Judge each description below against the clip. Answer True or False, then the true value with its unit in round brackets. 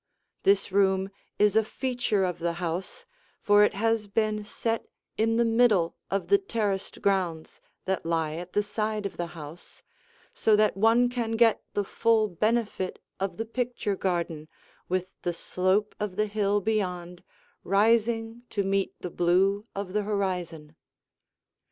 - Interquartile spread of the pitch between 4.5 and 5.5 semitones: False (3.4 semitones)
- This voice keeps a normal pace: True (150 wpm)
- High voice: True (200 Hz)